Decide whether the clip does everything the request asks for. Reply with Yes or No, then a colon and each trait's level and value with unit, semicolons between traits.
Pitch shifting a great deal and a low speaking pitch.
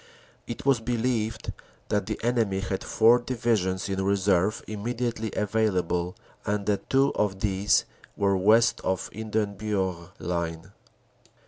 No: average, 2.9 semitones; low, 105 Hz